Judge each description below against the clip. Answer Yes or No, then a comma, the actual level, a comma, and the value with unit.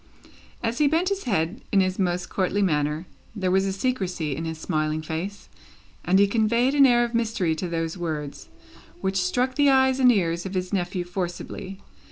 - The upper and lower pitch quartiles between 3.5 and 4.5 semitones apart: No, wide, 5.5 semitones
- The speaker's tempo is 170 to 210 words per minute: Yes, average, 190 wpm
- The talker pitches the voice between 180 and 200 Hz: Yes, high, 190 Hz